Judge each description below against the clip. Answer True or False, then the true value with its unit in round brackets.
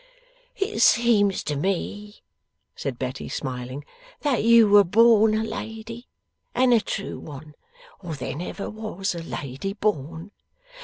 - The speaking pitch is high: True (200 Hz)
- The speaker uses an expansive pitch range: True (6.6 semitones)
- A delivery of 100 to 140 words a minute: True (135 wpm)